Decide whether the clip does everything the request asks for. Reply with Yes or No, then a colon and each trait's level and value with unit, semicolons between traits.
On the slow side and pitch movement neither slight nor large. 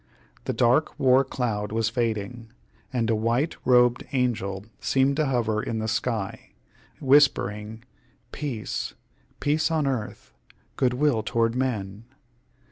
Yes: slow, 125 wpm; average, 3.3 semitones